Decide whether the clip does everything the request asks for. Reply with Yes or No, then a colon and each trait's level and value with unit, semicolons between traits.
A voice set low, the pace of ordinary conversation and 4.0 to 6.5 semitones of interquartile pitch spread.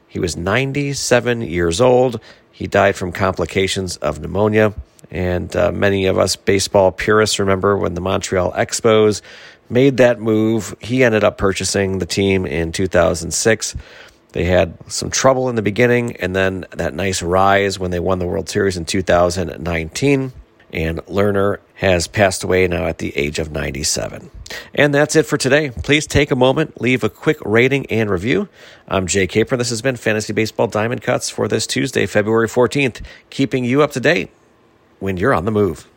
Yes: low, 100 Hz; average, 175 wpm; average, 4.9 semitones